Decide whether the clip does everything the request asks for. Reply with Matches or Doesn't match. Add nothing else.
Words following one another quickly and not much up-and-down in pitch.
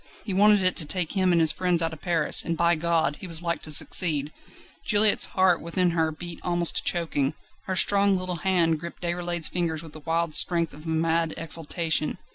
Matches